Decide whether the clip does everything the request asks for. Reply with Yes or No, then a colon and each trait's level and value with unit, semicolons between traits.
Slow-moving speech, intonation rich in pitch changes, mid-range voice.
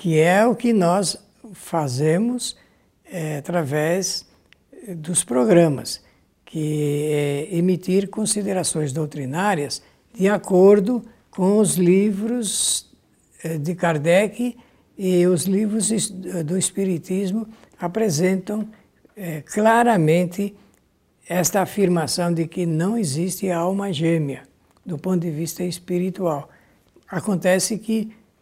No: slow, 100 wpm; average, 3.8 semitones; medium, 180 Hz